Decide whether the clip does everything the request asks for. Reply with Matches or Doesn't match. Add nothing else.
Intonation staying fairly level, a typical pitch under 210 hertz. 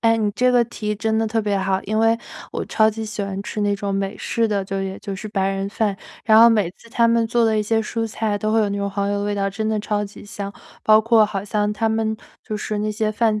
Doesn't match